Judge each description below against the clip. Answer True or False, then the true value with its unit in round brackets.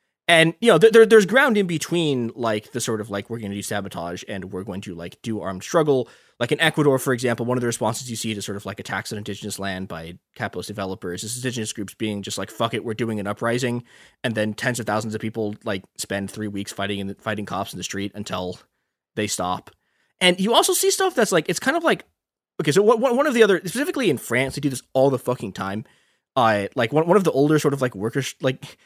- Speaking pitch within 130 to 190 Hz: False (115 Hz)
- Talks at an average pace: False (250 wpm)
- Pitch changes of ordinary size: False (6.2 semitones)